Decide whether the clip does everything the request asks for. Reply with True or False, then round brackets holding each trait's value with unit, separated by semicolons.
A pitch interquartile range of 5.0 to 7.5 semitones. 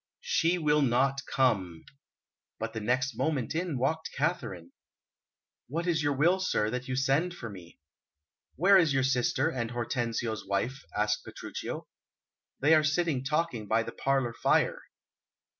True (5.4 semitones)